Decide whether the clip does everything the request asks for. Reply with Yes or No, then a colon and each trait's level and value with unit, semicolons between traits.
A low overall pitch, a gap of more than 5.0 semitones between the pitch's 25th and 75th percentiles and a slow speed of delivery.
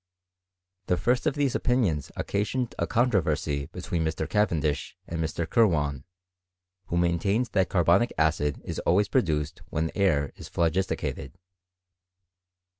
Yes: very low, 85 Hz; wide, 5.5 semitones; slow, 125 wpm